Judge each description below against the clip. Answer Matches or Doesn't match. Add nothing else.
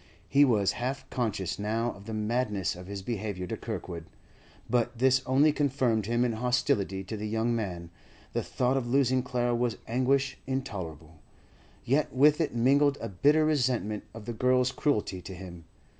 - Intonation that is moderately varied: Matches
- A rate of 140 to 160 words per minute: Doesn't match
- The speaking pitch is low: Matches